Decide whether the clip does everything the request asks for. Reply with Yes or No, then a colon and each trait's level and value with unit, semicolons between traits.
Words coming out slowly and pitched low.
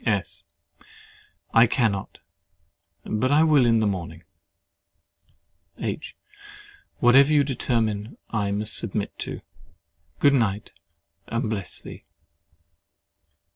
Yes: slow, 95 wpm; low, 115 Hz